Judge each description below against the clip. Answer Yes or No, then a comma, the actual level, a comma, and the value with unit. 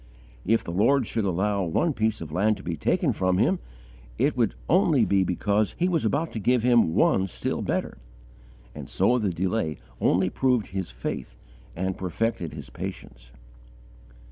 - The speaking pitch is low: Yes, low, 100 Hz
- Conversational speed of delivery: Yes, average, 170 wpm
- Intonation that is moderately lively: Yes, average, 4.5 semitones